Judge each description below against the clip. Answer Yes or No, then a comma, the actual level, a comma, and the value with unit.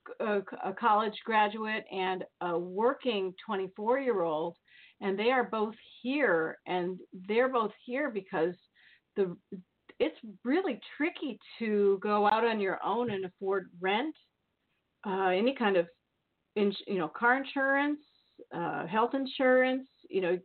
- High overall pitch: Yes, high, 215 Hz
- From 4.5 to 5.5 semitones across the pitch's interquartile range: Yes, average, 4.9 semitones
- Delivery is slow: Yes, slow, 130 wpm